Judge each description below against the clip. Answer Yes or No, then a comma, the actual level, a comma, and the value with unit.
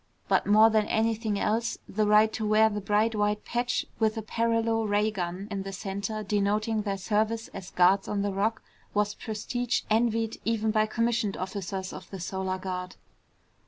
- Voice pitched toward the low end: No, high, 210 Hz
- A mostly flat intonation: Yes, narrow, 2.0 semitones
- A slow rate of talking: No, average, 175 wpm